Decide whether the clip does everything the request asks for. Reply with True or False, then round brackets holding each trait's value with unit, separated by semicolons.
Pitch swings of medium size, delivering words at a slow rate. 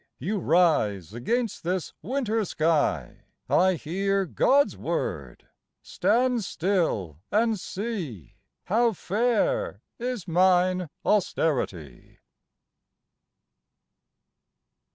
False (6.0 semitones; 75 wpm)